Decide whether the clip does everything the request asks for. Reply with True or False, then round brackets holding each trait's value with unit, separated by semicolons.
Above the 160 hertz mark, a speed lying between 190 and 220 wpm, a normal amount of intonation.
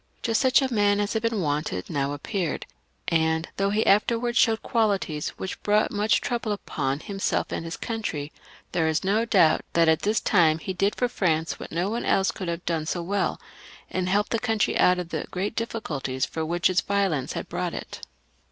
True (190 Hz; 200 wpm; 4.9 semitones)